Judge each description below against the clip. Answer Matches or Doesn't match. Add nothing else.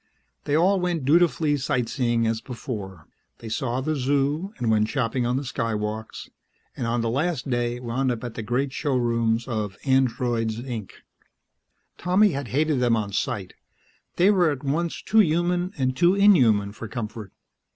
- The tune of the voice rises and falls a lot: Doesn't match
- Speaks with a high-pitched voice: Doesn't match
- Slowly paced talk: Doesn't match